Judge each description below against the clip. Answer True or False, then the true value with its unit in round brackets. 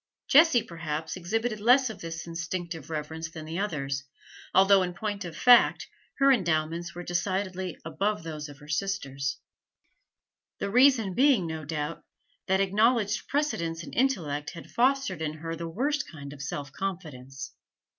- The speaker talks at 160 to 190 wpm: False (150 wpm)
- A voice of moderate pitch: True (175 Hz)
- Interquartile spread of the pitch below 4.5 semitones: False (5.1 semitones)